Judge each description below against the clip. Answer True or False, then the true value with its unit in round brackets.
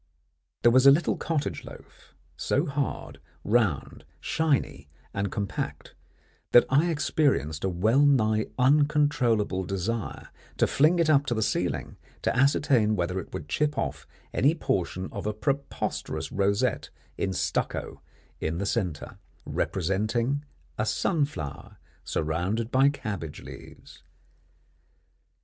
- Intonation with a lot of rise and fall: True (6.8 semitones)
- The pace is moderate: False (125 wpm)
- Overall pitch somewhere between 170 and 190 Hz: False (115 Hz)